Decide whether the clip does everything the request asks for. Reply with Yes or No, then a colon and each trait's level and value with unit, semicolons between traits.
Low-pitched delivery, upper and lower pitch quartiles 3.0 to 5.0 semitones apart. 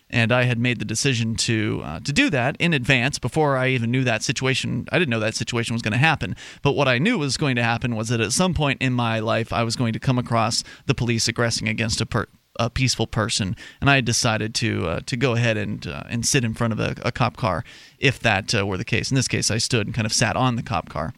No: low, 120 Hz; narrow, 2.5 semitones